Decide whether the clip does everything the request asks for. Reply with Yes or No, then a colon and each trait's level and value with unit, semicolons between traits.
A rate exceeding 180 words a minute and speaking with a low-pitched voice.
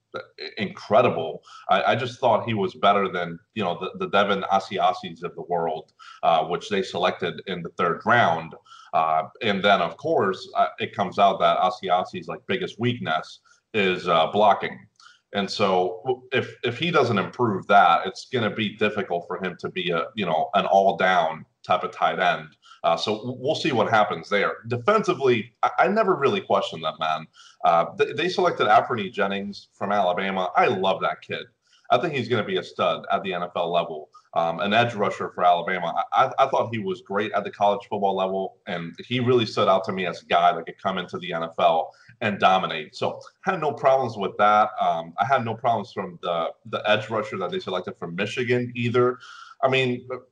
Yes: average, 200 wpm; low, 125 Hz